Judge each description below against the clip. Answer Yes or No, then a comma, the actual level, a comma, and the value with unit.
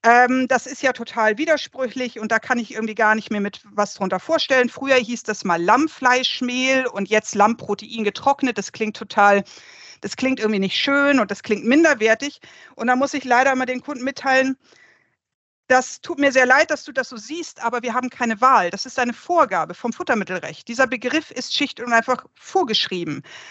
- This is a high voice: Yes, very high, 250 Hz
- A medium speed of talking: No, fast, 195 wpm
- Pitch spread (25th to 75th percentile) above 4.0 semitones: No, average, 3.4 semitones